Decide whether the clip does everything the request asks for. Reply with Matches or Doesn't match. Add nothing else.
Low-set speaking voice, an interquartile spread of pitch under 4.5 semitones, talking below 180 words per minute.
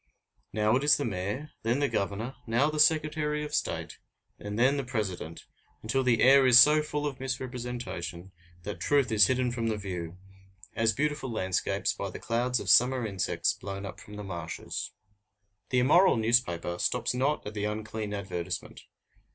Doesn't match